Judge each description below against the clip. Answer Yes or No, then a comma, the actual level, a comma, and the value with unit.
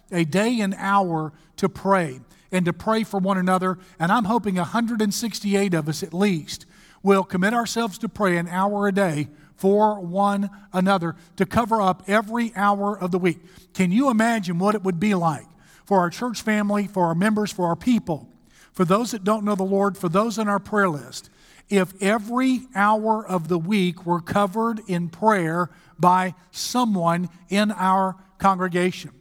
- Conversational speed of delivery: Yes, average, 175 wpm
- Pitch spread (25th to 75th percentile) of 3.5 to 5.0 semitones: No, average, 3.0 semitones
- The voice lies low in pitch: No, high, 195 Hz